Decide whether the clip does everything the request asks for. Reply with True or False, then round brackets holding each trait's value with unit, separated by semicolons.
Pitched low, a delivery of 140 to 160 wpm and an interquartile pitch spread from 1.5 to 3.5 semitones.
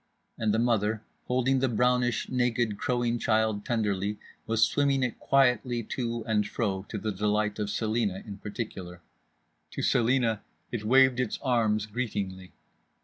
True (115 Hz; 145 wpm; 2.8 semitones)